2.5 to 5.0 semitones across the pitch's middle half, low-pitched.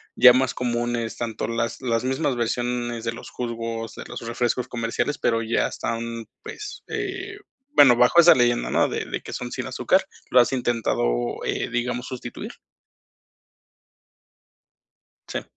No: narrow, 1.7 semitones; low, 120 Hz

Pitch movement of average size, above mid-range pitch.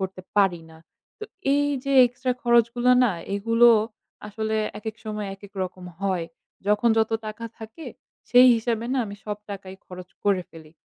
Yes: average, 3.5 semitones; high, 215 Hz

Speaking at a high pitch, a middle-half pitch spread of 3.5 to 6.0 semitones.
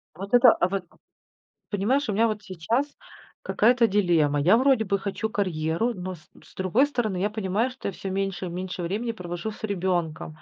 Yes: high, 195 Hz; average, 3.9 semitones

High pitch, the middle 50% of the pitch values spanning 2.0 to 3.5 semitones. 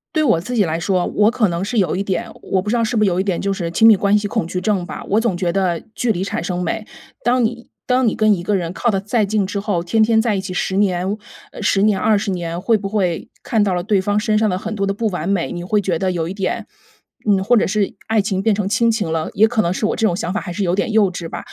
Yes: high, 200 Hz; average, 3.0 semitones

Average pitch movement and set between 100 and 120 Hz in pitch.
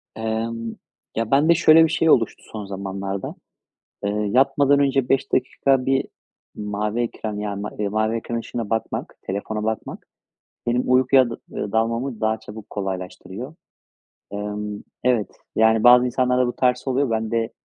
Yes: average, 3.4 semitones; low, 115 Hz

